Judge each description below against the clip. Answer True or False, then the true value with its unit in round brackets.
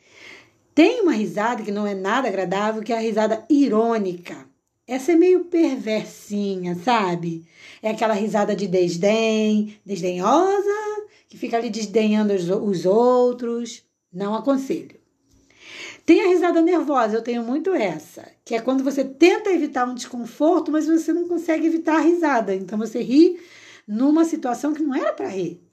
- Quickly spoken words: False (150 wpm)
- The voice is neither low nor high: False (240 Hz)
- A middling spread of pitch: False (7.3 semitones)